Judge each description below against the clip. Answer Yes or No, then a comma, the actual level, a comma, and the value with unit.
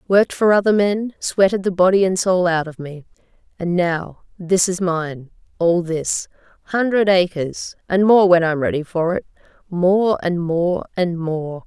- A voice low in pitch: No, medium, 180 Hz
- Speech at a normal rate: Yes, average, 170 wpm